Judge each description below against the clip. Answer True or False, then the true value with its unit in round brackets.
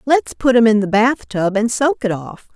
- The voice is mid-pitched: False (230 Hz)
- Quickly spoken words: True (260 wpm)